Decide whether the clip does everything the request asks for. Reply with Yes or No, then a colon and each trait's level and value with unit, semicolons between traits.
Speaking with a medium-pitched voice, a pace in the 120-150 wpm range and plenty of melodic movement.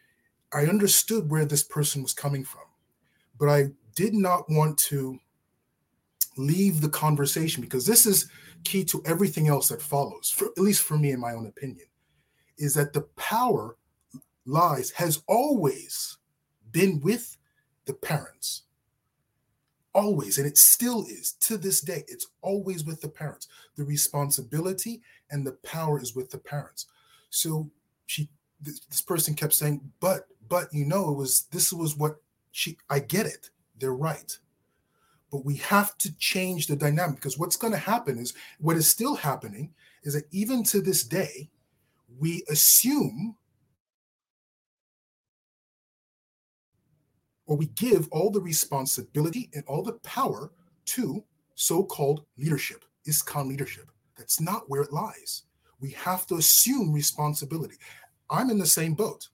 No: medium, 155 Hz; average, 145 wpm; average, 4.6 semitones